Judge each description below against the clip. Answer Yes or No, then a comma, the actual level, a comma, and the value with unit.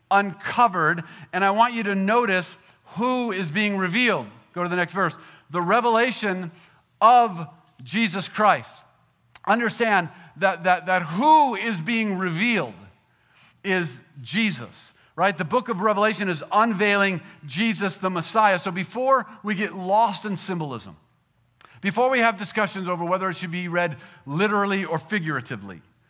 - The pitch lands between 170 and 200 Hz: Yes, high, 190 Hz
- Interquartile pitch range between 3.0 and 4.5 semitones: Yes, average, 3.8 semitones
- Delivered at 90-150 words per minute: Yes, average, 140 wpm